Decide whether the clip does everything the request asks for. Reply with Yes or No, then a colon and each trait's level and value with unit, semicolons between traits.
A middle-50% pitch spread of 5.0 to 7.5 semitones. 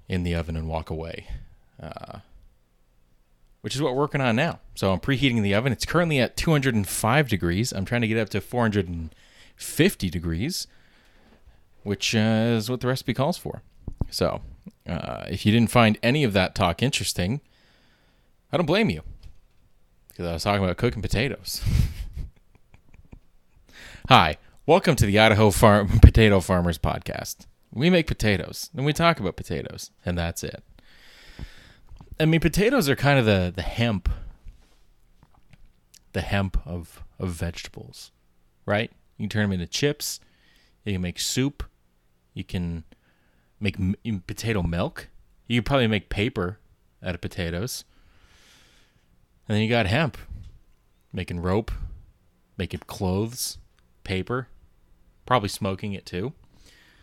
Yes: average, 5.3 semitones